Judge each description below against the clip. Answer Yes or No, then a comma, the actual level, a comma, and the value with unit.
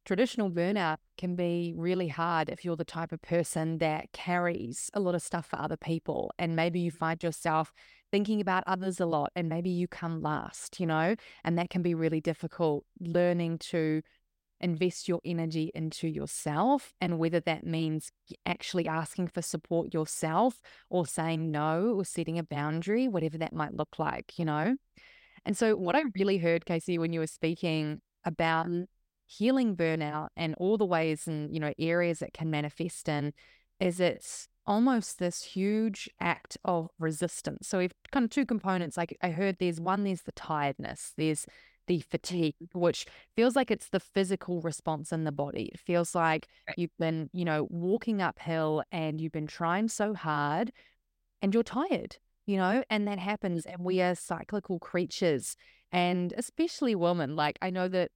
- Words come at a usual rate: Yes, average, 175 wpm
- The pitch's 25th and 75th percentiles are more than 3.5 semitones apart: No, average, 2.8 semitones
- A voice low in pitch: No, medium, 170 Hz